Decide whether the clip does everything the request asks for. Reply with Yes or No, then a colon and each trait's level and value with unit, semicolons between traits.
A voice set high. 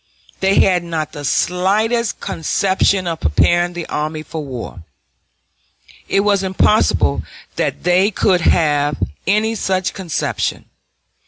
No: medium, 180 Hz